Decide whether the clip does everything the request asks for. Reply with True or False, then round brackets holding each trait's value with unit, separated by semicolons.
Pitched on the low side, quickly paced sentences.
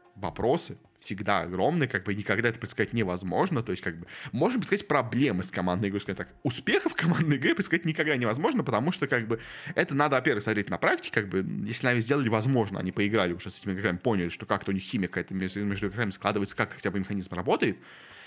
True (105 Hz; 210 wpm)